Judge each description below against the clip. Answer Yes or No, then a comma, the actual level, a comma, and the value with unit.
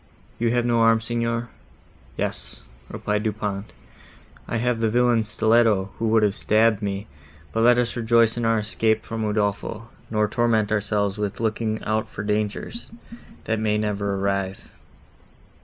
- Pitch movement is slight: Yes, narrow, 1.8 semitones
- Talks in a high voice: No, low, 110 Hz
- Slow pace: No, average, 150 wpm